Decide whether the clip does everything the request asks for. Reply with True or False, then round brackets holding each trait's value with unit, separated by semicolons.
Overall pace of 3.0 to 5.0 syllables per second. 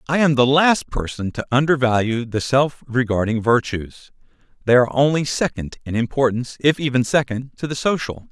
False (5.3 syllables/s)